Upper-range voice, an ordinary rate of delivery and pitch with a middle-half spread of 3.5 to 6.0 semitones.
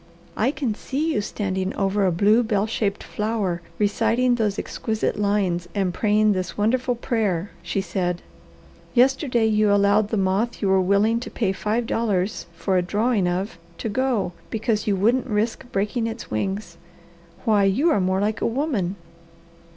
No: high, 210 Hz; average, 165 wpm; average, 3.0 semitones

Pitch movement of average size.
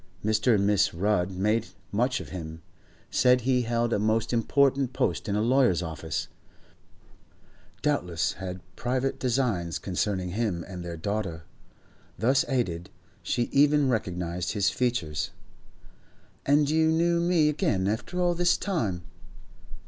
No: wide, 6.7 semitones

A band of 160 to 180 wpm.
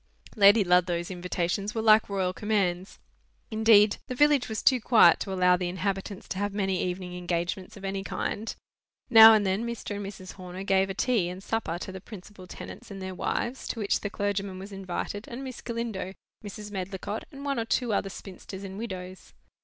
No: average, 195 wpm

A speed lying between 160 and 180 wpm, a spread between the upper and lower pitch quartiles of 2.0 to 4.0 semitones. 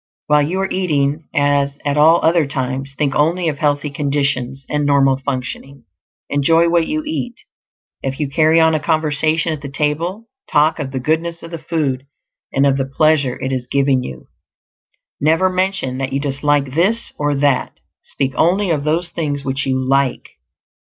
Yes: average, 175 wpm; average, 2.9 semitones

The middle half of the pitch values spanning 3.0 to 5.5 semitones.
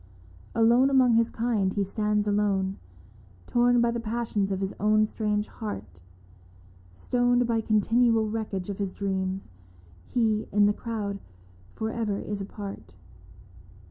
No: narrow, 2.6 semitones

